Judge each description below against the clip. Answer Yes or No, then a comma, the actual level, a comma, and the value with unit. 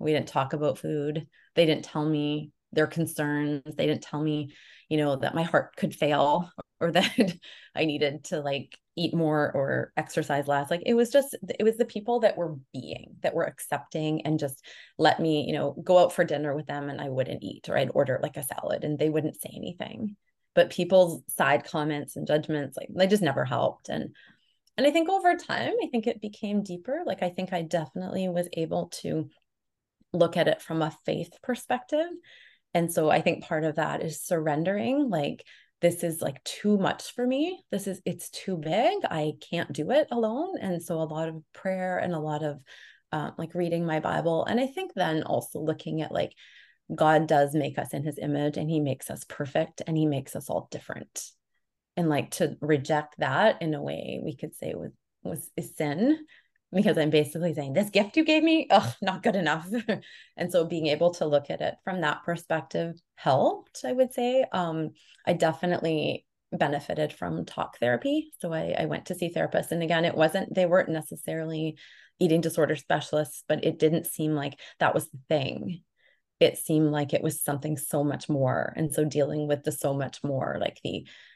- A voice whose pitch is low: No, medium, 160 Hz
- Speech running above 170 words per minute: Yes, average, 200 wpm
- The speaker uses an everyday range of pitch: Yes, average, 3.8 semitones